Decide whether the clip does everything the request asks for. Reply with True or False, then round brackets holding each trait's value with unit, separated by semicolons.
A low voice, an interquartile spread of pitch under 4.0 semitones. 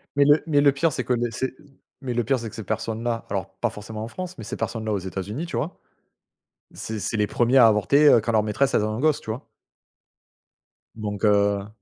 False (115 Hz; 4.3 semitones)